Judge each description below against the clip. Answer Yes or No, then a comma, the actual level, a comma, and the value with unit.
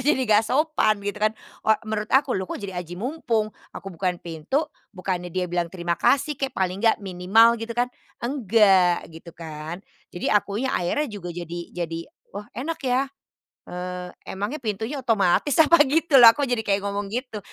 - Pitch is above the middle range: Yes, high, 210 Hz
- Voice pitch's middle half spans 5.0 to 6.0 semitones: Yes, wide, 5.6 semitones